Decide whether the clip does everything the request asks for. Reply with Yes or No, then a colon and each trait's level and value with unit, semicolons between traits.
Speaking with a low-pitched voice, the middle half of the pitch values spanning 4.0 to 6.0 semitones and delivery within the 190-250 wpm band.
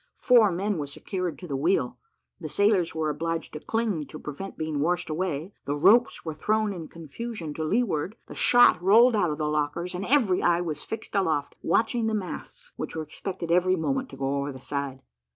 No: medium, 175 Hz; wide, 5.5 semitones; fast, 205 wpm